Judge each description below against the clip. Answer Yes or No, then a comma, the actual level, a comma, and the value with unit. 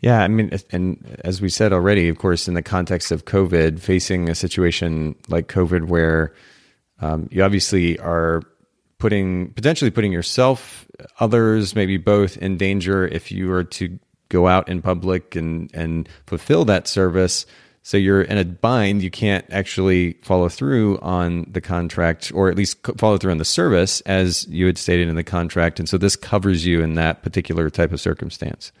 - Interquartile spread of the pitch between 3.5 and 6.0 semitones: No, narrow, 2.5 semitones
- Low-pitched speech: Yes, very low, 90 Hz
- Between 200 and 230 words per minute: No, average, 180 wpm